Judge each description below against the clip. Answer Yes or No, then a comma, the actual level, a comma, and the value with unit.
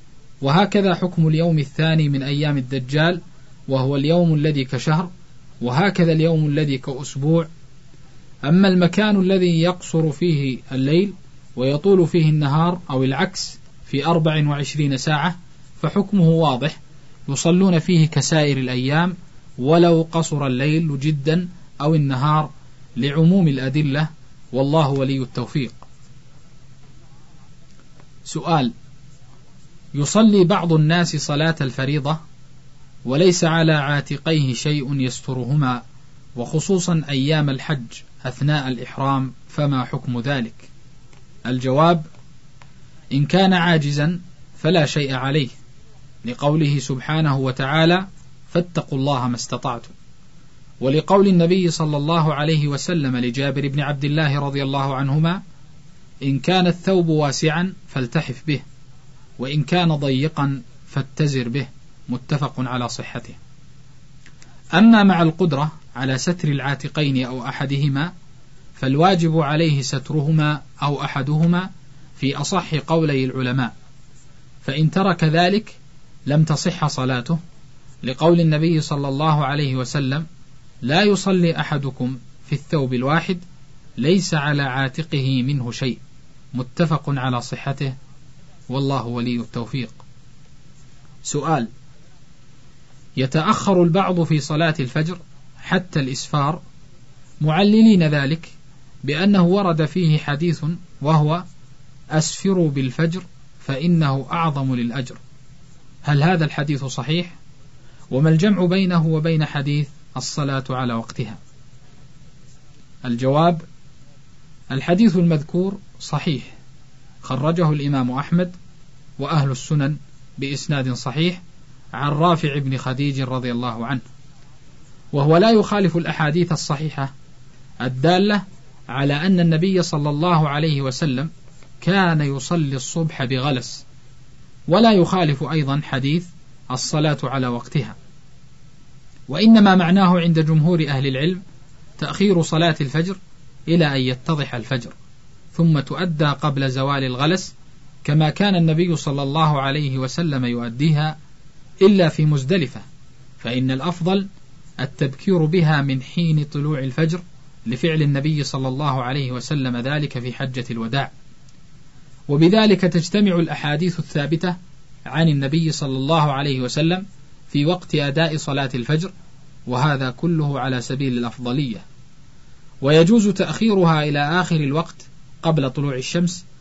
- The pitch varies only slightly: No, average, 3.4 semitones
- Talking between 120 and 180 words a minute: No, average, 100 wpm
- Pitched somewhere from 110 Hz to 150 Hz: Yes, medium, 145 Hz